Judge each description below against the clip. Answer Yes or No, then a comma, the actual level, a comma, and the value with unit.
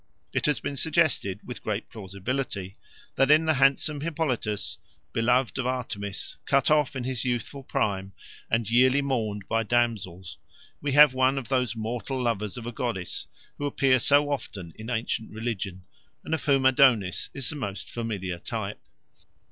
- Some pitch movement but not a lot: Yes, average, 4.5 semitones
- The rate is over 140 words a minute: Yes, average, 160 wpm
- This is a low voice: Yes, low, 120 Hz